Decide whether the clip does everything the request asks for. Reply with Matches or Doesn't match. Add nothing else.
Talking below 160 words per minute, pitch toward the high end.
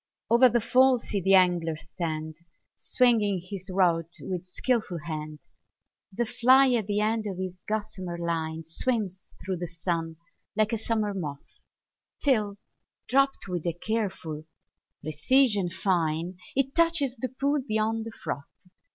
Matches